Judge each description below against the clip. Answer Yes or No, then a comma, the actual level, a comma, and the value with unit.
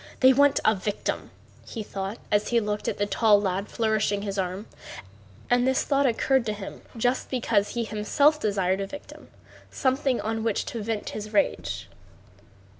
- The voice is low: No, high, 220 Hz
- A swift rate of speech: No, average, 170 wpm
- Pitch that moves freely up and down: No, average, 3.4 semitones